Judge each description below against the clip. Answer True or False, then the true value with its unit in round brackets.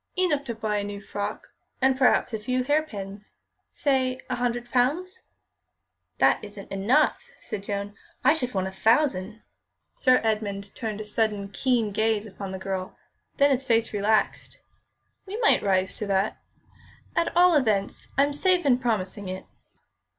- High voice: True (220 Hz)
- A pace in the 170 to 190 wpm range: False (155 wpm)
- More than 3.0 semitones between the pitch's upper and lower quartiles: True (4.7 semitones)